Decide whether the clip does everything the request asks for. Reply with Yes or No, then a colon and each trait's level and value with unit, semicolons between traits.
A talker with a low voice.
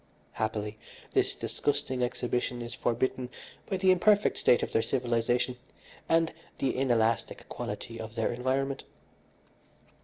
Yes: low, 125 Hz